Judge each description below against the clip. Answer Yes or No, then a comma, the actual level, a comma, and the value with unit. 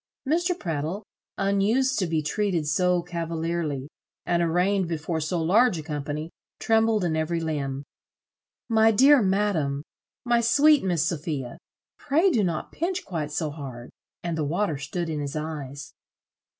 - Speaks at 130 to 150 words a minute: Yes, average, 145 wpm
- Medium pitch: Yes, medium, 170 Hz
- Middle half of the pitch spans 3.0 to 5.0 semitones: No, wide, 5.4 semitones